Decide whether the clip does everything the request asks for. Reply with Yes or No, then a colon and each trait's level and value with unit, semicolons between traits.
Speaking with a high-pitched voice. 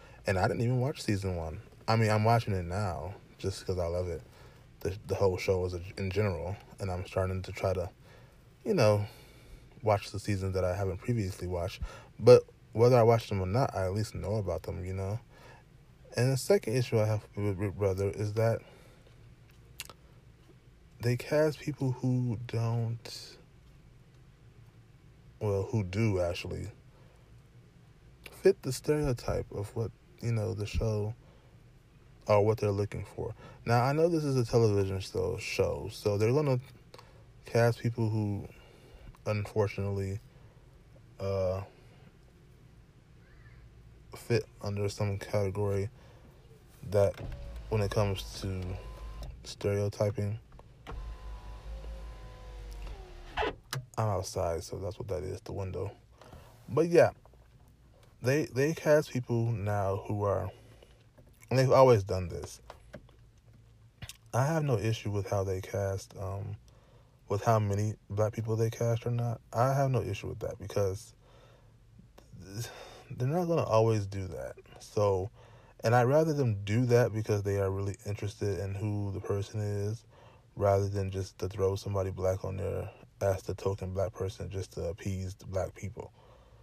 No: low, 110 Hz